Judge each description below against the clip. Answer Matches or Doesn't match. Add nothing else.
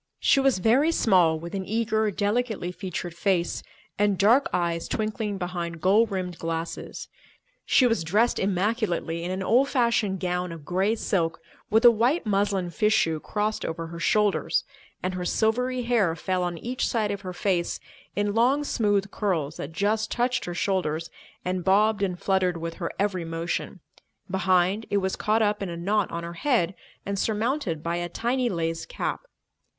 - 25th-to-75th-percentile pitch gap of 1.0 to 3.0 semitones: Doesn't match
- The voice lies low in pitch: Doesn't match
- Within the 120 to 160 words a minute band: Doesn't match